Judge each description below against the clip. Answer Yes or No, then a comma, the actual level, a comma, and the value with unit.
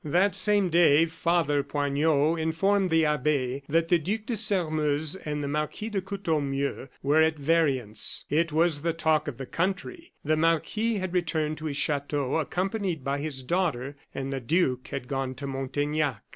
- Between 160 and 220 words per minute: Yes, average, 170 wpm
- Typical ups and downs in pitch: Yes, average, 3.5 semitones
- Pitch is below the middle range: No, medium, 155 Hz